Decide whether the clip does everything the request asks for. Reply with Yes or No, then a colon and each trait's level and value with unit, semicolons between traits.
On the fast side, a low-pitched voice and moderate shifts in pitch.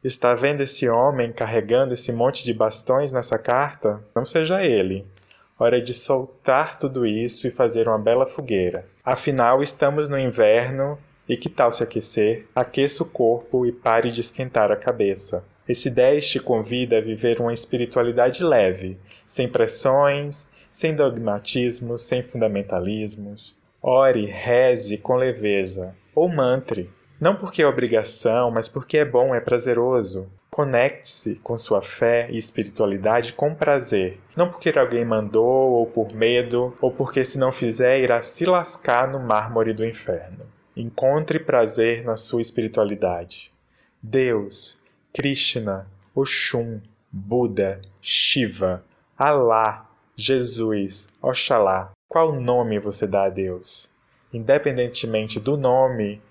No: average, 130 wpm; low, 120 Hz; average, 3.4 semitones